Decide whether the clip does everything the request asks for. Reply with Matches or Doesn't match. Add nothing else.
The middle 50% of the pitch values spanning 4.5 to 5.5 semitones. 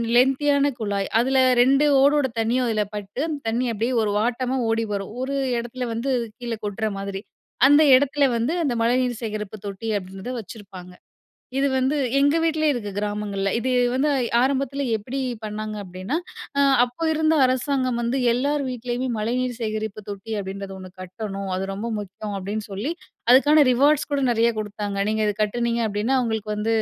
Doesn't match